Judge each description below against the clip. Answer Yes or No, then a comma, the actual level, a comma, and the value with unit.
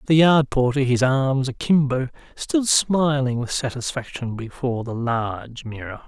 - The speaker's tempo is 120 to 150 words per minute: Yes, average, 140 wpm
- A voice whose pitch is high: No, low, 130 Hz